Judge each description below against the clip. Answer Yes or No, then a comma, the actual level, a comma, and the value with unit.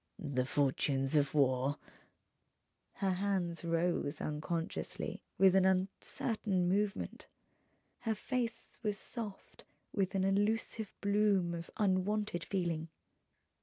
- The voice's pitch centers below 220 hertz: Yes, medium, 185 Hz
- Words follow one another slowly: Yes, slow, 105 wpm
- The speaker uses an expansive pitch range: No, average, 3.8 semitones